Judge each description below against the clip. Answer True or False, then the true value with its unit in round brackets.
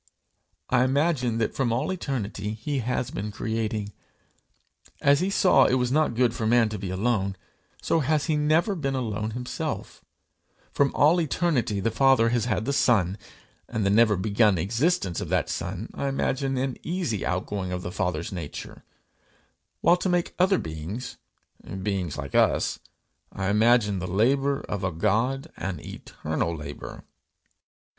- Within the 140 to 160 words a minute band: True (155 wpm)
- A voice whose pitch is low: True (115 Hz)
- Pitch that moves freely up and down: True (5.7 semitones)